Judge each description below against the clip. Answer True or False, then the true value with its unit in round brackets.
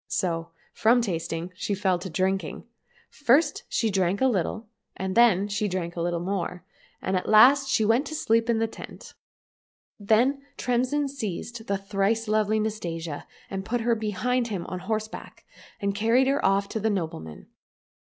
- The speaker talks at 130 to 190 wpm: True (165 wpm)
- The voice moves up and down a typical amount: True (3.8 semitones)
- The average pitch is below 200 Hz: False (210 Hz)